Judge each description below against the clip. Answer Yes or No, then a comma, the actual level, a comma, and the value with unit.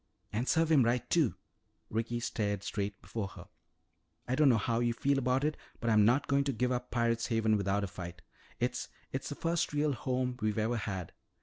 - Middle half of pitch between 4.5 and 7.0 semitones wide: No, average, 3.5 semitones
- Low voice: Yes, low, 120 Hz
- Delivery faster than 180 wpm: Yes, fast, 205 wpm